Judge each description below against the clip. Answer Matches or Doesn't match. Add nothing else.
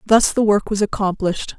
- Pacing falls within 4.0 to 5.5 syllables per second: Doesn't match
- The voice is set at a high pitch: Matches